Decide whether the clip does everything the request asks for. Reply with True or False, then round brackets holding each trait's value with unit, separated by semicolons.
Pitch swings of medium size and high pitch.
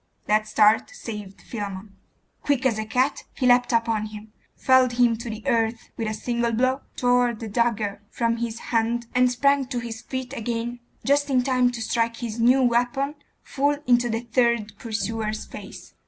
False (2.1 semitones; 235 Hz)